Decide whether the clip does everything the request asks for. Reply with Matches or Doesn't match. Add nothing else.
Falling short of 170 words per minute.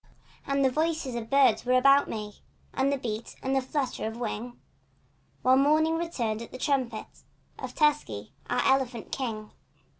Matches